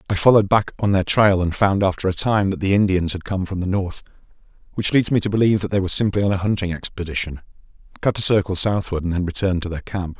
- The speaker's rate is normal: No, fast, 245 wpm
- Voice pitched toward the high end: No, very low, 95 Hz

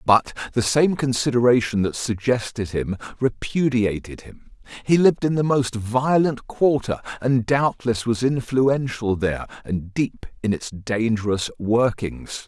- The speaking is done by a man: Yes, male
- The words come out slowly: Yes, slow, 130 wpm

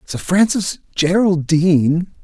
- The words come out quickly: No, slow, 80 wpm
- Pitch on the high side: No, medium, 180 Hz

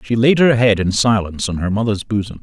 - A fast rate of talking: Yes, fast, 245 wpm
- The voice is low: Yes, low, 110 Hz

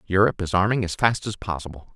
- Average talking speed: No, fast, 215 wpm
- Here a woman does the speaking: No, male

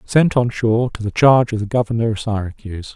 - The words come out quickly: Yes, fast, 225 wpm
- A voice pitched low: Yes, low, 115 Hz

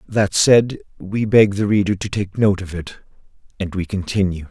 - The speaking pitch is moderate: No, low, 100 Hz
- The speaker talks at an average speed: Yes, average, 185 wpm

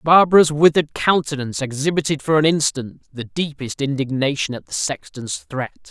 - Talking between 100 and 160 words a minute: Yes, average, 140 wpm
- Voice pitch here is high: No, medium, 145 Hz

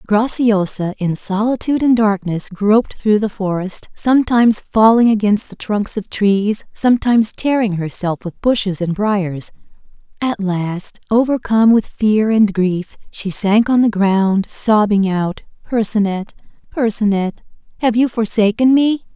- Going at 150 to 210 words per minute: No, slow, 135 wpm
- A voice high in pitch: Yes, high, 210 Hz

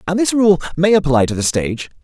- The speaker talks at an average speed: No, fast, 235 wpm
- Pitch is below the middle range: No, medium, 165 Hz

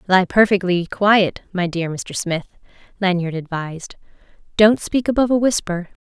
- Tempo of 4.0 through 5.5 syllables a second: Yes, 4.9 syllables/s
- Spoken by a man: No, female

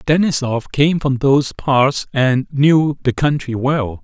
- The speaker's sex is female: No, male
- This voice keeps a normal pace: Yes, average, 150 wpm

